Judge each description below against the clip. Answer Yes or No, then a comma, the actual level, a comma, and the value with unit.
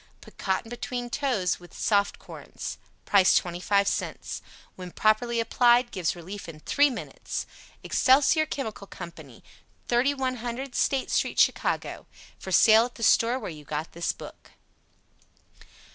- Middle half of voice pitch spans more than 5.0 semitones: Yes, wide, 5.4 semitones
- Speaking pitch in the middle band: No, high, 220 Hz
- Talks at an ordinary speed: No, slow, 130 wpm